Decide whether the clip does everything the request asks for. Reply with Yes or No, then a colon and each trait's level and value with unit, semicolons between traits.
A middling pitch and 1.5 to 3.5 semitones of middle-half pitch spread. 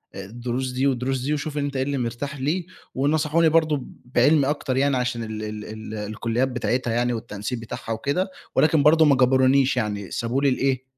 No: low, 130 Hz; average, 3.2 semitones